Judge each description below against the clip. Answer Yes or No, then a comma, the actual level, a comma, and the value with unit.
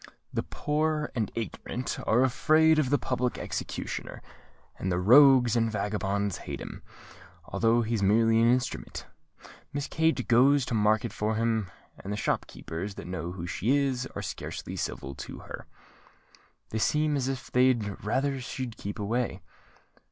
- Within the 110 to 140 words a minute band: No, average, 155 wpm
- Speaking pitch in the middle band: No, low, 115 Hz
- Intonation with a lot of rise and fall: No, average, 4.2 semitones